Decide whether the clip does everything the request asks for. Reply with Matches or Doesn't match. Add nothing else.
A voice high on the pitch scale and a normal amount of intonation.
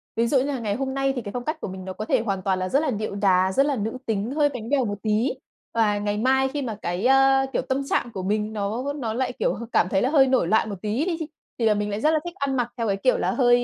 Matches